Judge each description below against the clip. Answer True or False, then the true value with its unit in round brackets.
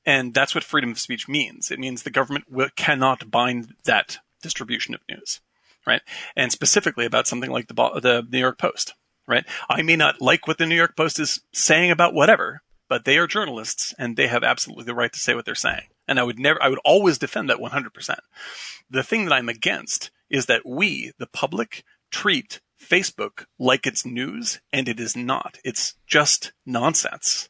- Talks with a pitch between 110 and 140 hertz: True (135 Hz)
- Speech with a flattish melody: False (3.4 semitones)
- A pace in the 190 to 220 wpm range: True (195 wpm)